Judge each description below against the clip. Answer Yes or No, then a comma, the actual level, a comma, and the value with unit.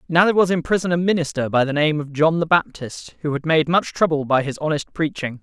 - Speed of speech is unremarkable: No, fast, 255 wpm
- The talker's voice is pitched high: No, medium, 155 Hz